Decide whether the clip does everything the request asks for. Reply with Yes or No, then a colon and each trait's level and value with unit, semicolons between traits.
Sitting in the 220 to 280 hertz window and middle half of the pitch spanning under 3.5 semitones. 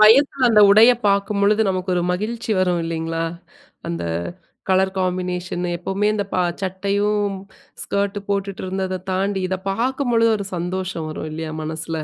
No: high, 190 Hz; narrow, 2.5 semitones